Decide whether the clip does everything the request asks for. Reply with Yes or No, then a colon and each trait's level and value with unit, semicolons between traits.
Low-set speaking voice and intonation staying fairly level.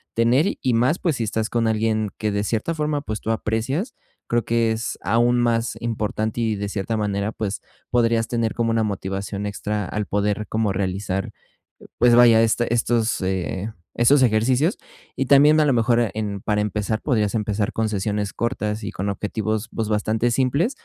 Yes: low, 110 Hz; narrow, 2.2 semitones